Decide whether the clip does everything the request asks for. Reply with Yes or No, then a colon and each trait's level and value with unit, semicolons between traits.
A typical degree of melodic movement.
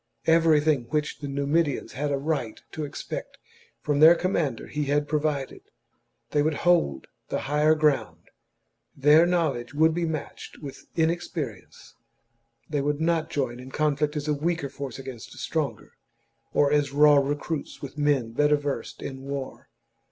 No: narrow, 2.1 semitones